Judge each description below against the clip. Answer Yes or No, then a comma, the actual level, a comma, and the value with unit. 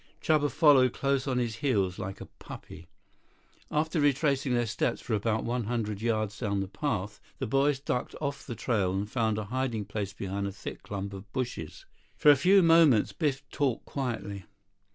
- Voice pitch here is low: Yes, low, 120 Hz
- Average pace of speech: Yes, average, 180 wpm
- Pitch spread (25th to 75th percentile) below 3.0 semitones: No, average, 5.2 semitones